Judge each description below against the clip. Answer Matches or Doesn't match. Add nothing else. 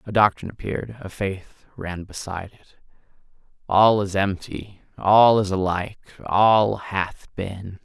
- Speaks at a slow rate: Matches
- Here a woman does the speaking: Doesn't match